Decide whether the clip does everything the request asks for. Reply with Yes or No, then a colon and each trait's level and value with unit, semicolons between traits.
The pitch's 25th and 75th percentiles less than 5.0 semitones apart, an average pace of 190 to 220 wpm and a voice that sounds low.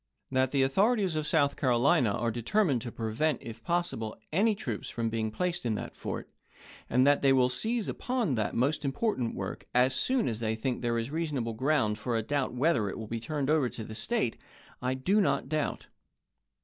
No: average, 5.3 semitones; average, 200 wpm; low, 130 Hz